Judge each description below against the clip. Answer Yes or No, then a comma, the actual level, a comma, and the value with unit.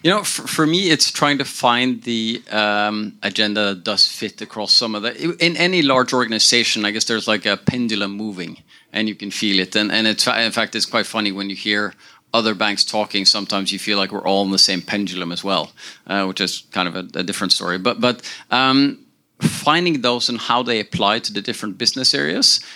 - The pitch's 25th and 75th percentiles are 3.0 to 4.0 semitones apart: Yes, average, 3.3 semitones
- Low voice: Yes, low, 110 Hz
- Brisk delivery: Yes, fast, 220 wpm